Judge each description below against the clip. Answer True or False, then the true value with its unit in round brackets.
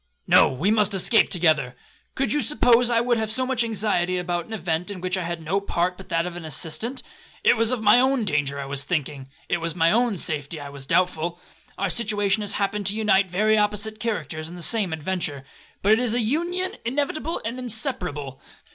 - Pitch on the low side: False (195 Hz)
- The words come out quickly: True (210 wpm)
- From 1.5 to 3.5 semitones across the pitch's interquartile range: False (5.4 semitones)